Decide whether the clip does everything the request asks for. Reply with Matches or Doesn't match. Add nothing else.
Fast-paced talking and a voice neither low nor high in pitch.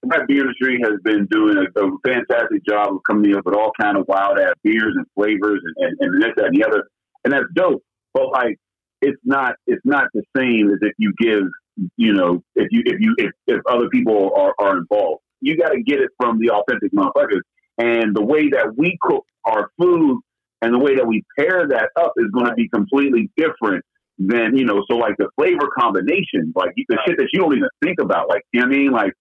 Matches